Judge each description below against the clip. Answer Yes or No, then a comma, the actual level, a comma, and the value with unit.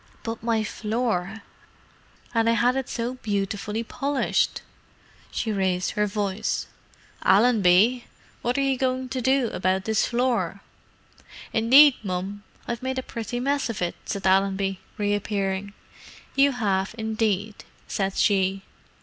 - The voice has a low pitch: No, high, 220 Hz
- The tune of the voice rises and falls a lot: No, average, 4.0 semitones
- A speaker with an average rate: No, slow, 130 wpm